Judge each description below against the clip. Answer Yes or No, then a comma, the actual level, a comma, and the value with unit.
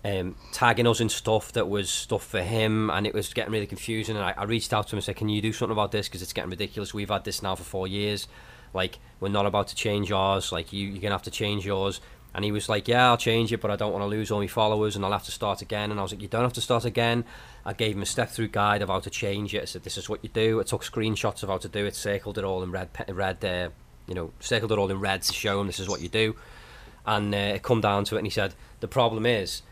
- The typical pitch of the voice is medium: No, low, 105 Hz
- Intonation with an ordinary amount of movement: No, narrow, 2.1 semitones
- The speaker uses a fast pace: Yes, fast, 305 wpm